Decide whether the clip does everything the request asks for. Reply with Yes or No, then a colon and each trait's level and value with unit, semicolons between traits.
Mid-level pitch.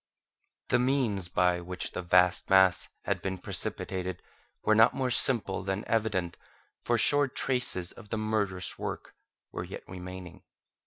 No: very low, 95 Hz